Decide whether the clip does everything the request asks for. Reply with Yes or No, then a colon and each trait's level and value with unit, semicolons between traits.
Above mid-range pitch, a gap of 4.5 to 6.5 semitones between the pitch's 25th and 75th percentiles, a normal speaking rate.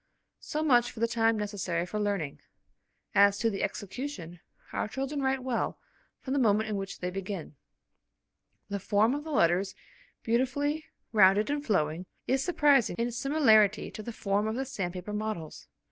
Yes: high, 215 Hz; average, 5.0 semitones; average, 165 wpm